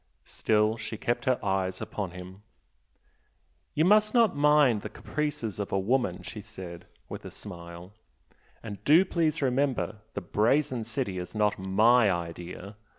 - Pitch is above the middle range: No, low, 110 Hz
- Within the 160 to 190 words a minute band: No, average, 150 wpm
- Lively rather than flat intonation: Yes, wide, 6.1 semitones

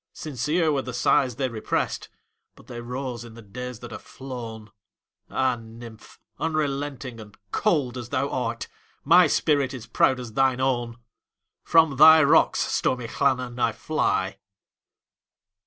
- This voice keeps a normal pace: No, slow, 125 wpm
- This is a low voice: Yes, low, 125 Hz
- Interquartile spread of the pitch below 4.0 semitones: Yes, average, 2.9 semitones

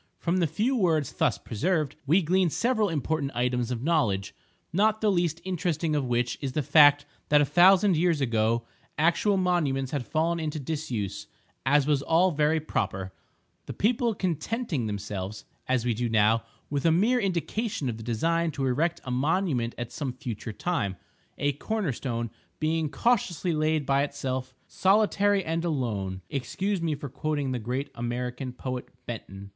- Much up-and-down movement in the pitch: Yes, wide, 5.9 semitones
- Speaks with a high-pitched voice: No, medium, 145 Hz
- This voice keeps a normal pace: Yes, average, 160 wpm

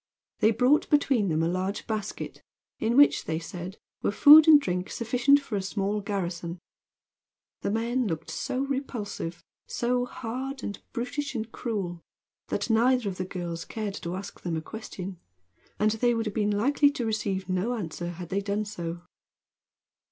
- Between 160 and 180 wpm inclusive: Yes, average, 165 wpm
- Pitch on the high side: Yes, high, 210 Hz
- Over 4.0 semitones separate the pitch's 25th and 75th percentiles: Yes, average, 4.9 semitones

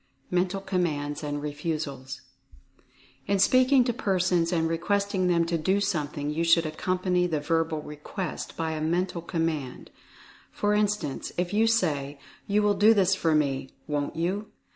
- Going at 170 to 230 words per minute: No, average, 150 wpm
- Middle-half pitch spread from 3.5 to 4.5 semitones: Yes, average, 4.2 semitones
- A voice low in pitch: No, medium, 170 Hz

